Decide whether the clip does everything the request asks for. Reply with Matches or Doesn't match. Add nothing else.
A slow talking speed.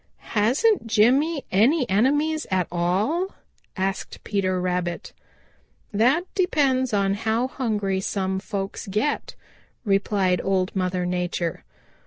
Matches